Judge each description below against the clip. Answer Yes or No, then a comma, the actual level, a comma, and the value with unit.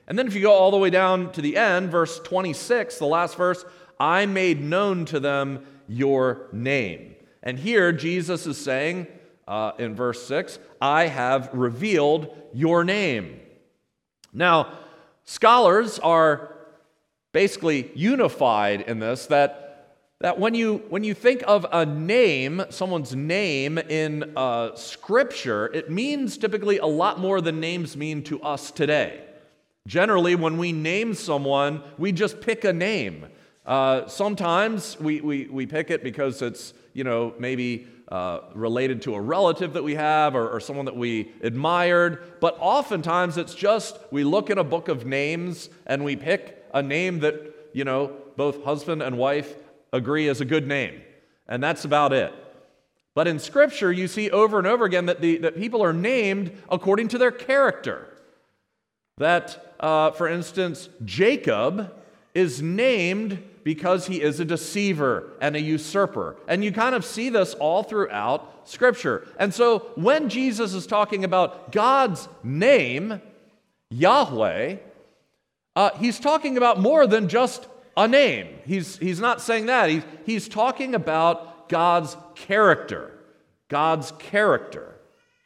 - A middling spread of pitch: No, wide, 5.7 semitones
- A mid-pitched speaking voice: Yes, medium, 170 Hz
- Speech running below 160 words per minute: Yes, average, 150 wpm